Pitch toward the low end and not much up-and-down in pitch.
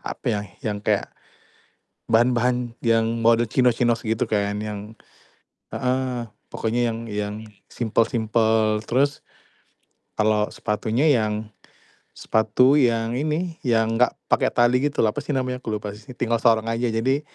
Yes: low, 115 Hz; narrow, 2.3 semitones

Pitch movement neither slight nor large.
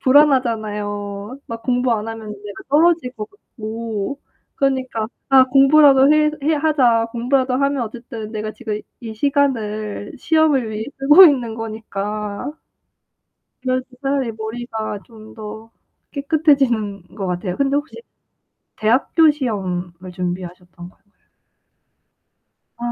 Yes: average, 4.5 semitones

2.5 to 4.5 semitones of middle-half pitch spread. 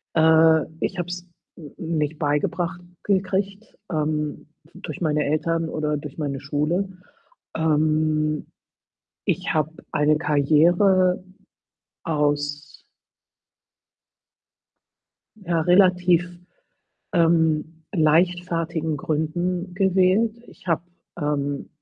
Yes: average, 2.8 semitones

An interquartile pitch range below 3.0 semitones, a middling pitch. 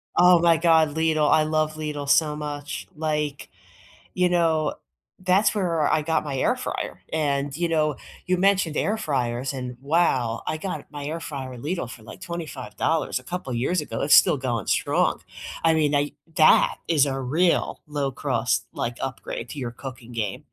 No: average, 3.4 semitones; medium, 150 Hz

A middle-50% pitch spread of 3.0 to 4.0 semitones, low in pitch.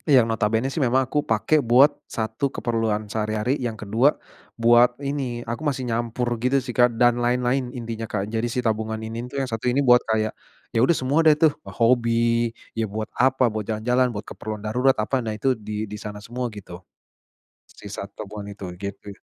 No: narrow, 2.6 semitones; low, 120 Hz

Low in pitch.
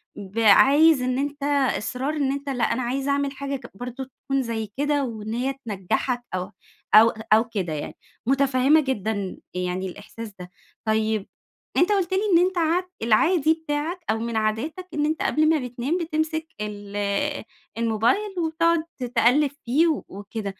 No: very high, 255 Hz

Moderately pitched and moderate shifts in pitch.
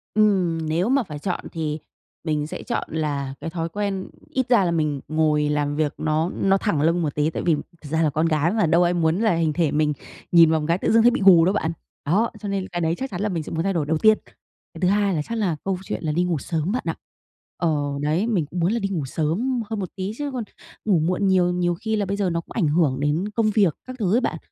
Yes: medium, 170 Hz; average, 4.3 semitones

